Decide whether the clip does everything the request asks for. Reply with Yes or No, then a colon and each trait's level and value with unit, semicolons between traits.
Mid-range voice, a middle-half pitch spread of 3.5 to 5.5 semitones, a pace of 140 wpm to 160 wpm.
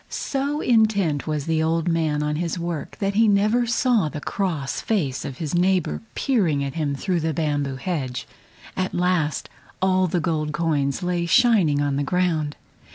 No: medium, 165 Hz; average, 4.2 semitones; average, 170 wpm